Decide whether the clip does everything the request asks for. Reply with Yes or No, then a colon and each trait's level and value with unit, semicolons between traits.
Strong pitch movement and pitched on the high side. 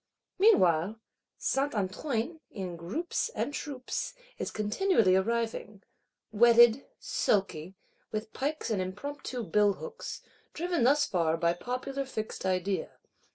Yes: wide, 6.5 semitones; high, 220 Hz